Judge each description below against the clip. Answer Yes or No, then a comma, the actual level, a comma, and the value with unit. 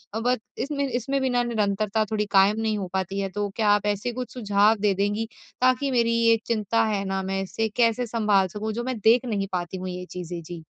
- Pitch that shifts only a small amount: No, average, 3.1 semitones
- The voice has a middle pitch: No, high, 210 Hz